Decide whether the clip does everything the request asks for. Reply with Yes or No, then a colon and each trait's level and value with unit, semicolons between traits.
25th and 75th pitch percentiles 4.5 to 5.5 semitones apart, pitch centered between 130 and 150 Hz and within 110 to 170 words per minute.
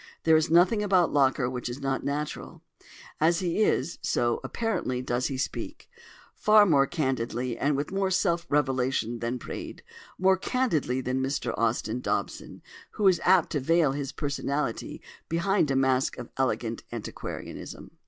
Yes: average, 5.2 semitones; medium, 140 Hz; average, 155 wpm